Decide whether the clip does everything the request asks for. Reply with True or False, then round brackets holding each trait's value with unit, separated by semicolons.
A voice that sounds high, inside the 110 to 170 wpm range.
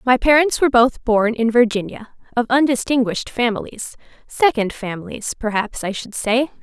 True (240 Hz; 135 wpm)